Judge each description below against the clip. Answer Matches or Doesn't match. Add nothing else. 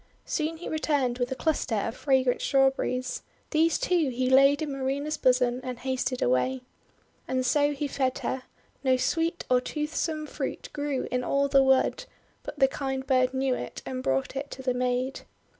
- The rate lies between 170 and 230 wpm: Matches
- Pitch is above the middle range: Matches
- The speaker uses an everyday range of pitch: Doesn't match